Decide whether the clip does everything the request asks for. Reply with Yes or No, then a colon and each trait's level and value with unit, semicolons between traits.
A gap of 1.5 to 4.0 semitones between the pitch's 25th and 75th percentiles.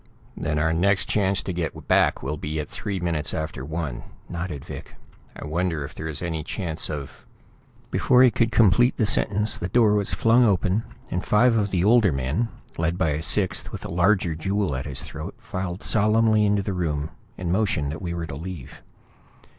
No: average, 4.8 semitones